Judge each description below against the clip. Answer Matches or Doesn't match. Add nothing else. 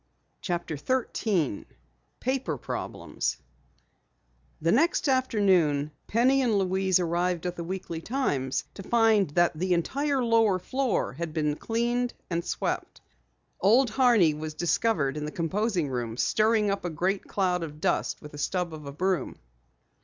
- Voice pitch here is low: Doesn't match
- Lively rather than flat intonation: Matches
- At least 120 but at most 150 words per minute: Matches